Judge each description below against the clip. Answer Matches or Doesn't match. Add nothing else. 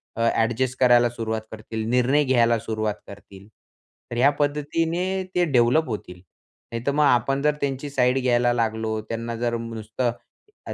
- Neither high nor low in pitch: Doesn't match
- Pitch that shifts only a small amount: Doesn't match